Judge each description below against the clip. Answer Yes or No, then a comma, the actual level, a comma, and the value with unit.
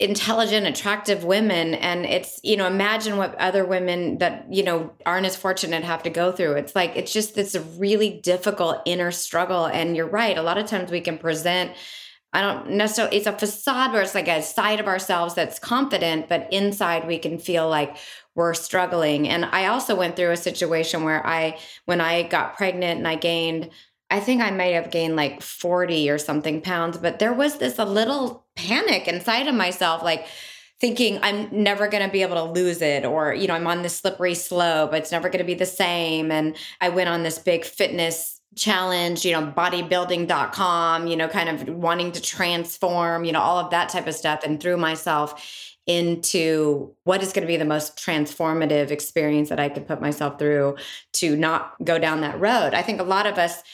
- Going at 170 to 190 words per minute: No, fast, 205 wpm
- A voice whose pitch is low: No, medium, 175 Hz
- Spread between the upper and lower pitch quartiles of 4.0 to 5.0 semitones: No, average, 3.0 semitones